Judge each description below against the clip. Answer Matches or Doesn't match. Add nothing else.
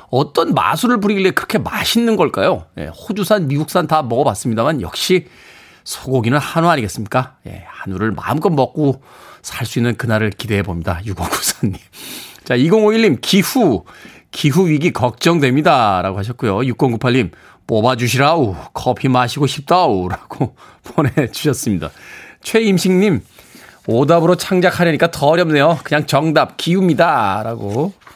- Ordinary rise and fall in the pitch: Doesn't match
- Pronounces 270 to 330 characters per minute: Matches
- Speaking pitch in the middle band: Matches